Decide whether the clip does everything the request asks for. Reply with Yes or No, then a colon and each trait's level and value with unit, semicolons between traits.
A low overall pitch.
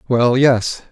Yes: low, 125 Hz